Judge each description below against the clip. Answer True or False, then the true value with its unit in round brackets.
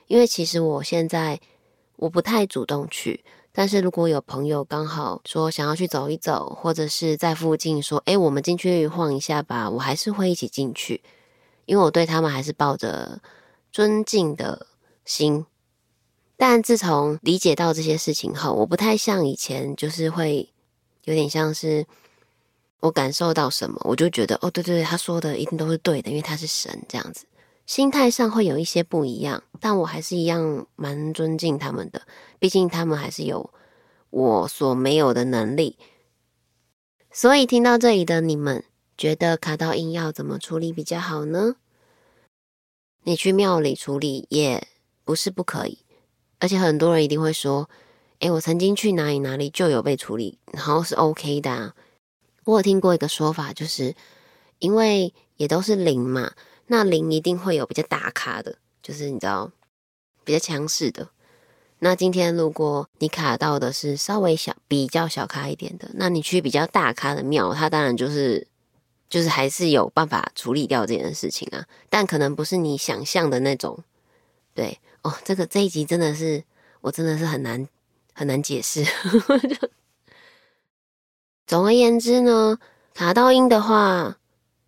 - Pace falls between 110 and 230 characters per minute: False (250 characters per minute)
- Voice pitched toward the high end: False (160 Hz)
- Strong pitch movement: False (3.9 semitones)